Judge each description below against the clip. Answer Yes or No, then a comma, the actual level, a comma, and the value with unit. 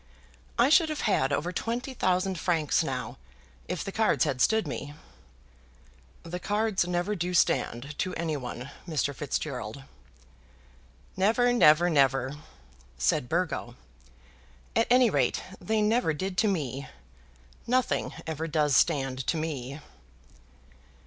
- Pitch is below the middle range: No, medium, 165 Hz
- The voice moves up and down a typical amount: No, wide, 6.7 semitones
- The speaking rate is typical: No, slow, 130 wpm